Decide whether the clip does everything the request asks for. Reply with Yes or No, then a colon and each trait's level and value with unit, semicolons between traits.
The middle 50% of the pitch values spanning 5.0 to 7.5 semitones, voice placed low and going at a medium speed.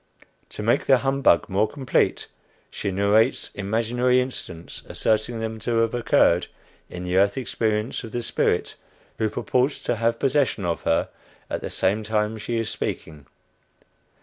No: average, 3.2 semitones; low, 110 Hz; average, 150 wpm